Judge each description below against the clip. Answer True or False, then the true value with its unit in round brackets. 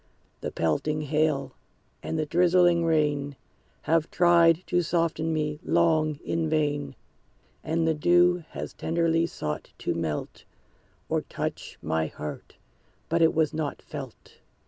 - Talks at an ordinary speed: False (130 wpm)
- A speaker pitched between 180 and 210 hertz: False (160 Hz)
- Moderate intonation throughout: False (2.3 semitones)